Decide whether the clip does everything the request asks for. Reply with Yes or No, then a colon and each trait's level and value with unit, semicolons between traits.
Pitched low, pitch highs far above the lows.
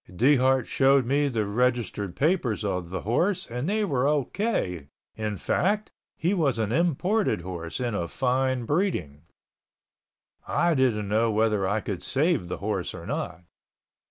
Yes: low, 125 Hz; wide, 6.5 semitones